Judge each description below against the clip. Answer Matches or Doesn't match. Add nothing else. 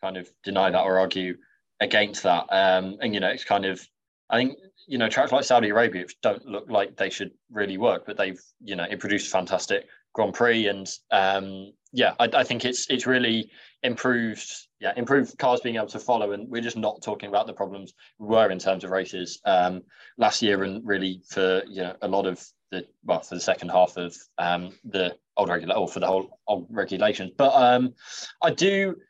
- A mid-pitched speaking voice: Doesn't match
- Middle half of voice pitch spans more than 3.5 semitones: Matches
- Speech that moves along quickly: Matches